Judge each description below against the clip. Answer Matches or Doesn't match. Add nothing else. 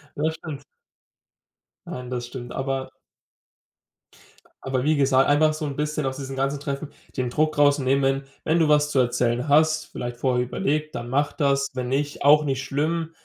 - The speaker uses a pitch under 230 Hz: Matches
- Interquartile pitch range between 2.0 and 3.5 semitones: Matches